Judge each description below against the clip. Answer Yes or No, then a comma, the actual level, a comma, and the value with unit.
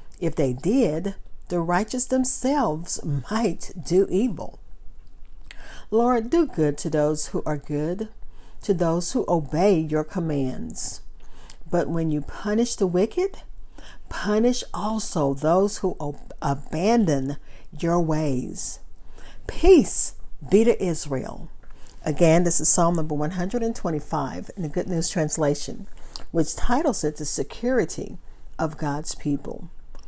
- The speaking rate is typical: No, slow, 120 wpm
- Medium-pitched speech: Yes, medium, 170 Hz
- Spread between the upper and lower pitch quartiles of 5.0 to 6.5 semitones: Yes, wide, 5.6 semitones